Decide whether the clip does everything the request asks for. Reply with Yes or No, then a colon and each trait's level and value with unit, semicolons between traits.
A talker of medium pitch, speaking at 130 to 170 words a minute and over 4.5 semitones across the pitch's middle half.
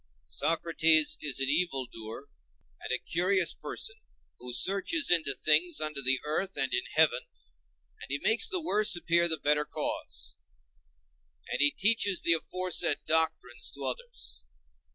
Yes: medium, 160 Hz; average, 145 wpm; average, 5.0 semitones